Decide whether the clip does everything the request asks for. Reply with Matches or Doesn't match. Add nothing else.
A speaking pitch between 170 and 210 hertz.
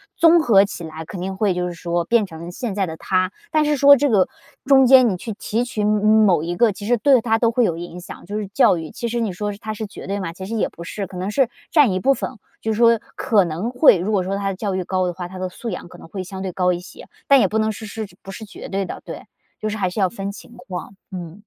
Matches